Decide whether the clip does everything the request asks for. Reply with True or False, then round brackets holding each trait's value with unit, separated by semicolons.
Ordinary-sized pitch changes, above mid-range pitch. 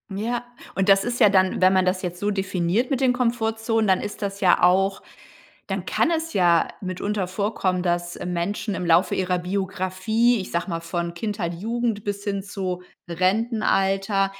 True (3.0 semitones; 195 Hz)